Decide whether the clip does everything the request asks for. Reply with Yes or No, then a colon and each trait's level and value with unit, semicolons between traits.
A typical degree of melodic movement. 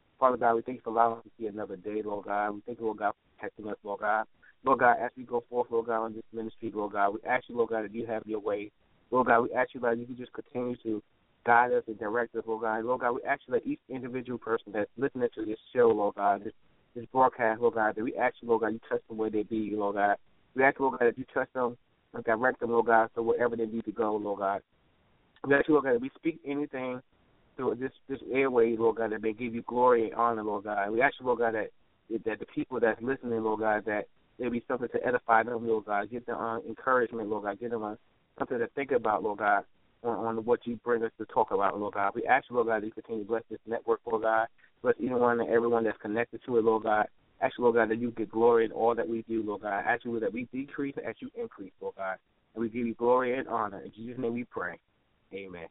No: narrow, 2.0 semitones